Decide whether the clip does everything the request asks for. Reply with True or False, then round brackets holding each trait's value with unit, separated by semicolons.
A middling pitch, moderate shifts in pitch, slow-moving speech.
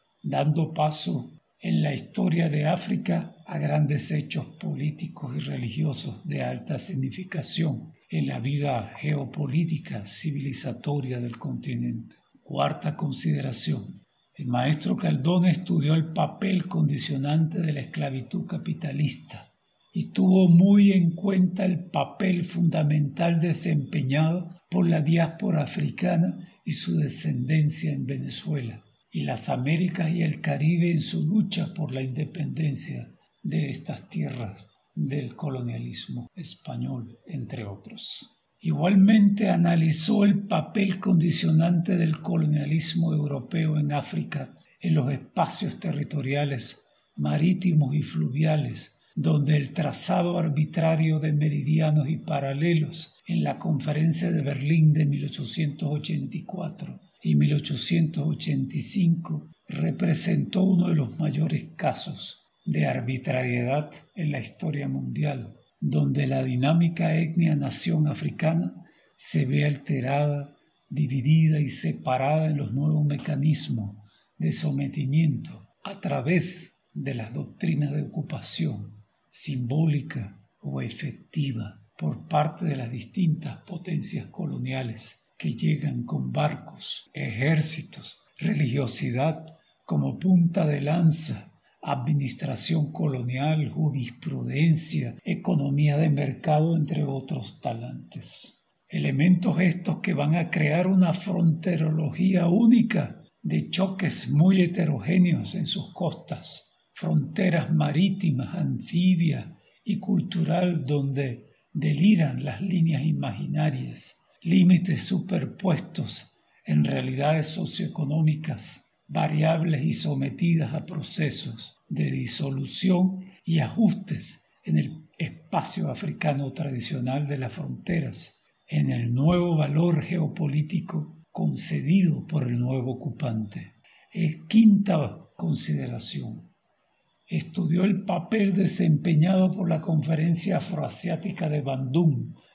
True (155 Hz; 3.3 semitones; 105 wpm)